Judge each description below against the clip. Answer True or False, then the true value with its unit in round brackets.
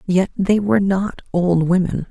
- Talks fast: False (170 wpm)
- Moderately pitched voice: True (180 Hz)